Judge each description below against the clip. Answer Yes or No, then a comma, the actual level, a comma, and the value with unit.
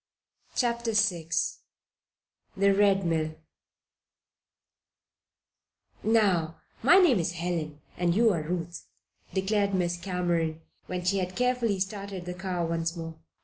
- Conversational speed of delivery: No, slow, 110 wpm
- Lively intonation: No, average, 3.4 semitones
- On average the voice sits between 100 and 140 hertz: No, medium, 180 Hz